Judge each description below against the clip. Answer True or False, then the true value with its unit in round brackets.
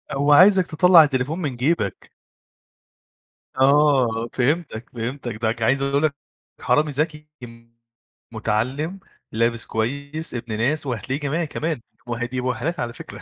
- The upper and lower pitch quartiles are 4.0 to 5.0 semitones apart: True (4.4 semitones)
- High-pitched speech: False (135 Hz)